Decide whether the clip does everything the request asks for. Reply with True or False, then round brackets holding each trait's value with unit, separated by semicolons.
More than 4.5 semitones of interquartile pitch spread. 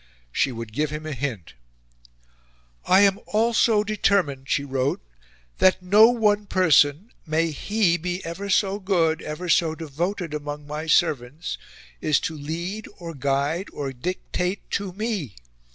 True (5.3 semitones)